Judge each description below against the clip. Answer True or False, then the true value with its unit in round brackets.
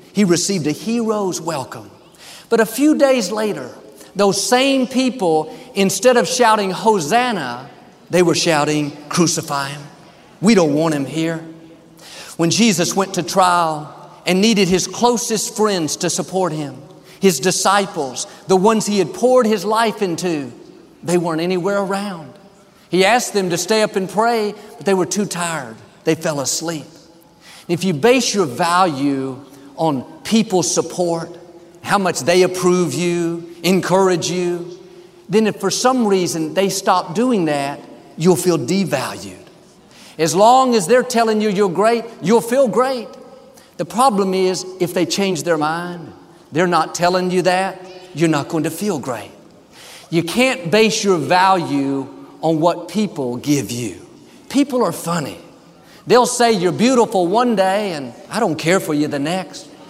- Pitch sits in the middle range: True (180 Hz)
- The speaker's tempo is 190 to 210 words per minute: False (155 wpm)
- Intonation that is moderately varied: True (4.2 semitones)